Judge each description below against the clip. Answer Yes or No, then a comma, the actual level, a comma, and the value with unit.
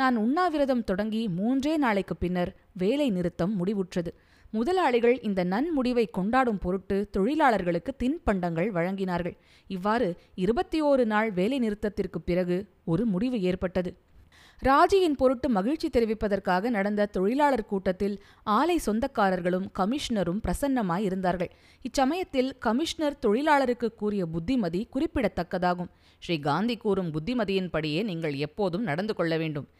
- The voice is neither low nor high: No, high, 210 Hz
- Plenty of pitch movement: Yes, wide, 5.8 semitones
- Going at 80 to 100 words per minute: No, average, 110 wpm